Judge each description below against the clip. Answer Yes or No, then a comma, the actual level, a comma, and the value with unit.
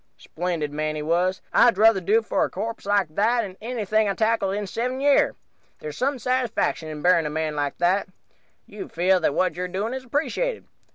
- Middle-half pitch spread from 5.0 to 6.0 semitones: Yes, average, 5.3 semitones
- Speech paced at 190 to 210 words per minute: Yes, average, 195 wpm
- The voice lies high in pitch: Yes, high, 195 Hz